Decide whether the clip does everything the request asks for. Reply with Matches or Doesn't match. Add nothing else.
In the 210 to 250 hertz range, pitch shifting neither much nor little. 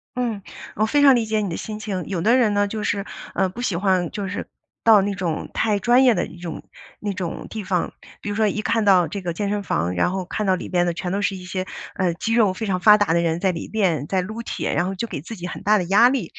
Doesn't match